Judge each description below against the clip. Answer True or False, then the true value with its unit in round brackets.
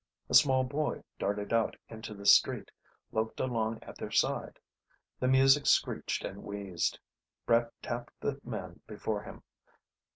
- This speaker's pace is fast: False (140 wpm)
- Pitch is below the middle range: True (115 Hz)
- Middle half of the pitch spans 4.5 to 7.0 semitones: False (4.1 semitones)